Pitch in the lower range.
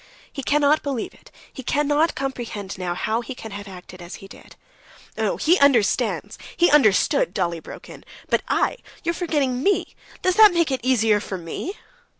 No: very high, 255 Hz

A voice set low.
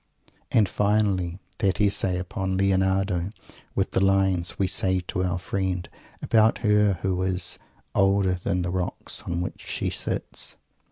Yes: very low, 95 Hz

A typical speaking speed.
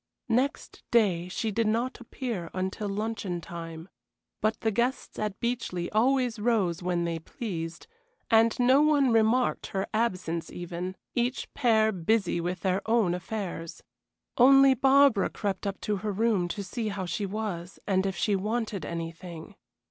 Yes: average, 150 wpm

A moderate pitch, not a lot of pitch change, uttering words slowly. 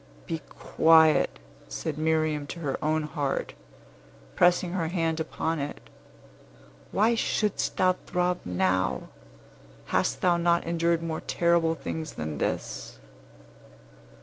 Yes: medium, 160 Hz; narrow, 2.3 semitones; slow, 120 wpm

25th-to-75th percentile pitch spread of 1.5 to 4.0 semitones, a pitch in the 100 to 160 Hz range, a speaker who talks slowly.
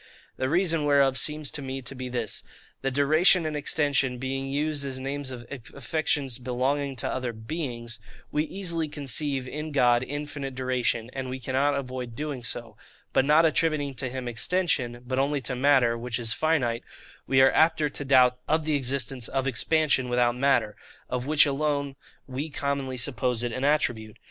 No: average, 2.8 semitones; low, 135 Hz; average, 170 wpm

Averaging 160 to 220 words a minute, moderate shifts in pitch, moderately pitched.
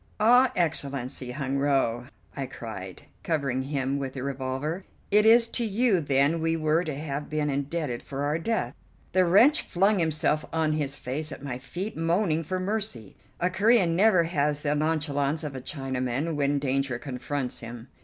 Yes: average, 170 wpm; average, 4.0 semitones; medium, 150 Hz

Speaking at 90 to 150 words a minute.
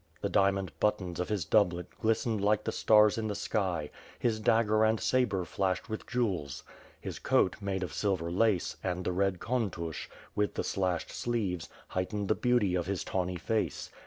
No: average, 175 wpm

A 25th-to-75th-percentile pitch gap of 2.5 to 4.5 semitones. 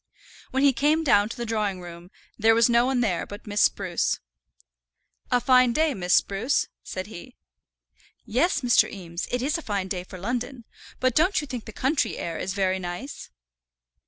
No: average, 5.3 semitones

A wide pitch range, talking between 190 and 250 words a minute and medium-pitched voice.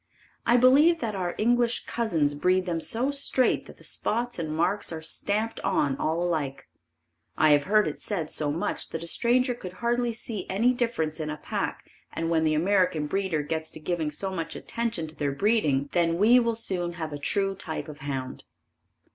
Yes: wide, 6.5 semitones; average, 195 wpm; medium, 180 Hz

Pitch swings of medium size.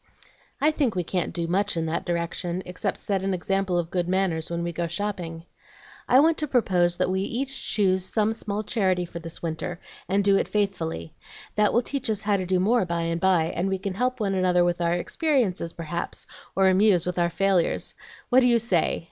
Yes: average, 3.3 semitones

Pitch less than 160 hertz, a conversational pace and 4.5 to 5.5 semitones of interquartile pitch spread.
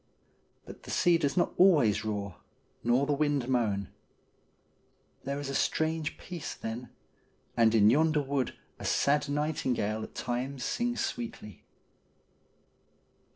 No: medium, 140 Hz; slow, 125 wpm; average, 5.2 semitones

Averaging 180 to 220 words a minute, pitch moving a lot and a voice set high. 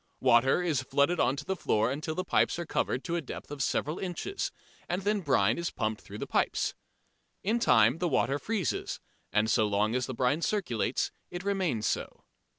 No: average, 195 wpm; wide, 6.4 semitones; medium, 145 Hz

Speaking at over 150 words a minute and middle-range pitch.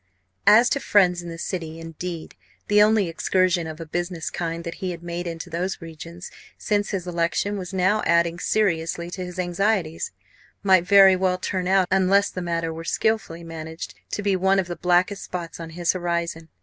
Yes: average, 190 wpm; medium, 175 Hz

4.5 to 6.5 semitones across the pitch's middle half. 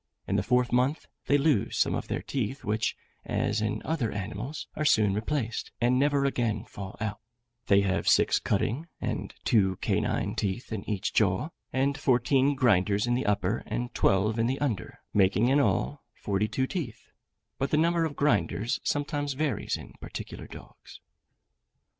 Yes: average, 5.1 semitones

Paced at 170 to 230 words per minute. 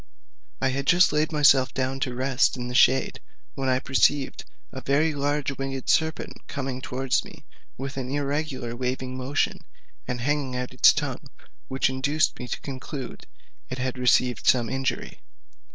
No: average, 160 wpm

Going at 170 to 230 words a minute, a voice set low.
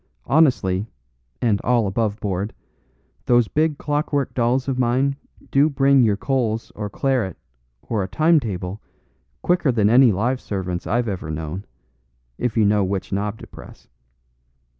No: average, 140 wpm; low, 115 Hz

